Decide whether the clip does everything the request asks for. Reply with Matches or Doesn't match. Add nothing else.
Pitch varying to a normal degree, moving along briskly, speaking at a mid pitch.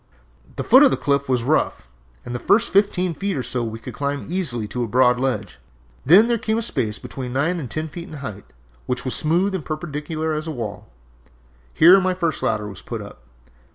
Doesn't match